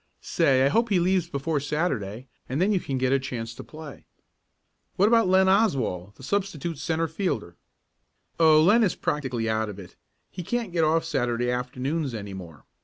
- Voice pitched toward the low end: No, medium, 145 Hz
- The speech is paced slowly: No, average, 180 wpm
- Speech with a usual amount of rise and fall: No, wide, 6.5 semitones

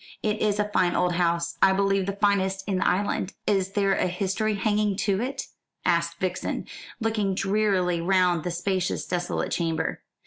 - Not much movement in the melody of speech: Yes, narrow, 2.3 semitones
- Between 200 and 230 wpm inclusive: No, average, 170 wpm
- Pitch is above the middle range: Yes, high, 195 Hz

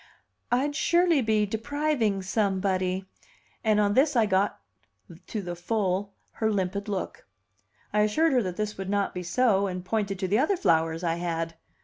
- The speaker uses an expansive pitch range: No, average, 3.3 semitones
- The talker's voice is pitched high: Yes, high, 205 Hz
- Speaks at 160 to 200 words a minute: Yes, average, 165 wpm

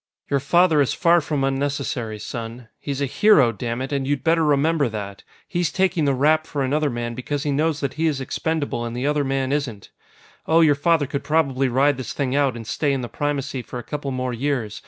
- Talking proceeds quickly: Yes, fast, 220 wpm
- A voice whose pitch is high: No, medium, 140 Hz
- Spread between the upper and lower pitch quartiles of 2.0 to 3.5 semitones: Yes, average, 2.9 semitones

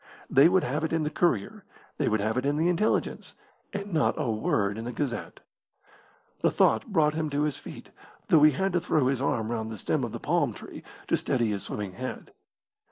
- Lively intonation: Yes, wide, 6.2 semitones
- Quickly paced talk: Yes, fast, 220 wpm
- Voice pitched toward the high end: No, medium, 140 Hz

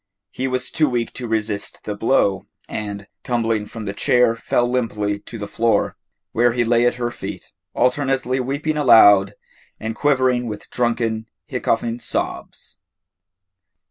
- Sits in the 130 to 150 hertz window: No, low, 115 Hz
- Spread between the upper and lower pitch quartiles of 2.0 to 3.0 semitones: Yes, average, 2.7 semitones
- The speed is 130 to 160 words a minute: Yes, average, 140 wpm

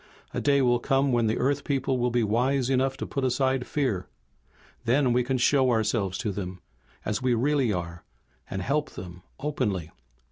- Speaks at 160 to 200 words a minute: Yes, average, 180 wpm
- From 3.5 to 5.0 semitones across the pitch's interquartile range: Yes, average, 4.1 semitones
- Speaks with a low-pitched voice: Yes, low, 125 Hz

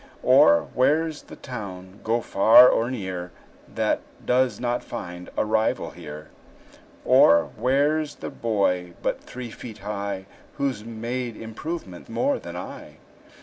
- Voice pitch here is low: Yes, low, 110 Hz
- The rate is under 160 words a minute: Yes, slow, 135 wpm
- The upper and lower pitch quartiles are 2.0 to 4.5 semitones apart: No, average, 5.2 semitones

